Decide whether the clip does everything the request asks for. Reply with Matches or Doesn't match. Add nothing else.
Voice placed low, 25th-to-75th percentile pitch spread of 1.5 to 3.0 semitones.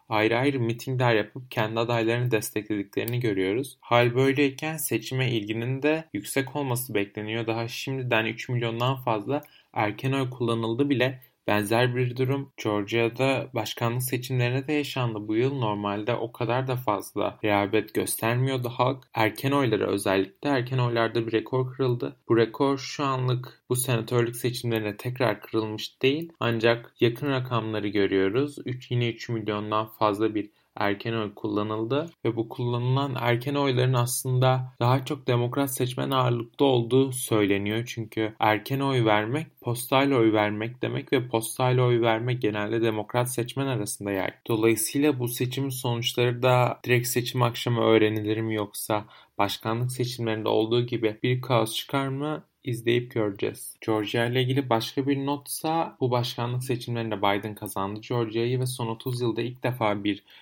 Matches